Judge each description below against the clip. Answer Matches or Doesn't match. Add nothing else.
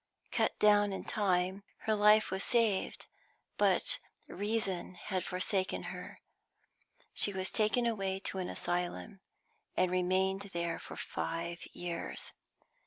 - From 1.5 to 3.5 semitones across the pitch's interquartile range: Matches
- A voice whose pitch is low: Doesn't match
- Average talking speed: Doesn't match